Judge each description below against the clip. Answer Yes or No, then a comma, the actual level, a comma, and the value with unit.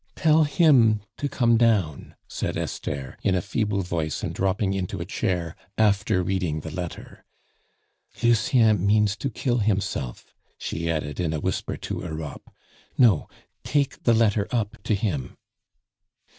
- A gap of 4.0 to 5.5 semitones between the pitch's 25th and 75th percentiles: Yes, average, 5.2 semitones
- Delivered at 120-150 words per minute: Yes, average, 145 wpm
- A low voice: Yes, low, 100 Hz